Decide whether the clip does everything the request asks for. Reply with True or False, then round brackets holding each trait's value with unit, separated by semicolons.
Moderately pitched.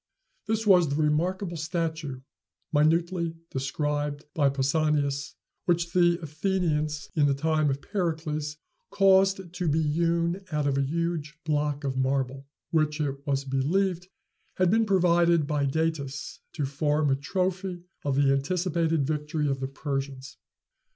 True (155 Hz)